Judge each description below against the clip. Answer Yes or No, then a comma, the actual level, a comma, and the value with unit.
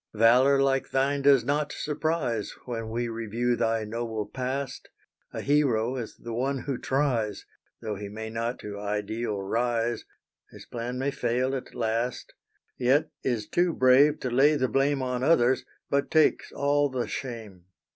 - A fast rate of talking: No, average, 155 wpm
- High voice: No, low, 125 Hz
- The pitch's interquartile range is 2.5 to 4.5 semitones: Yes, average, 3.3 semitones